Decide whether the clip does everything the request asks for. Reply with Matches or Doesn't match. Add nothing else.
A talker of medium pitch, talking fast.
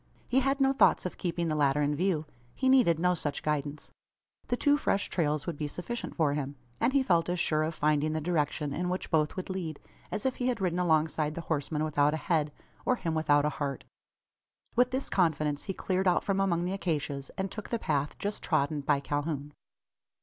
Matches